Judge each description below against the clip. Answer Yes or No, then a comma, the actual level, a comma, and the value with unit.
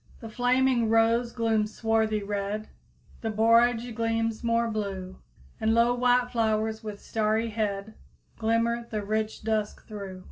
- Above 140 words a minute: No, slow, 135 wpm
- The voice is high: Yes, high, 225 Hz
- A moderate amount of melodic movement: No, narrow, 1.4 semitones